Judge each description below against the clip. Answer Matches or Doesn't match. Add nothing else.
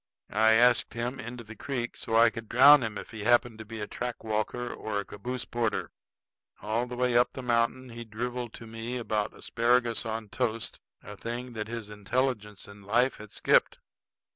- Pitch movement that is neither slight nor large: Doesn't match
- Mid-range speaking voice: Doesn't match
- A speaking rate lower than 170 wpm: Doesn't match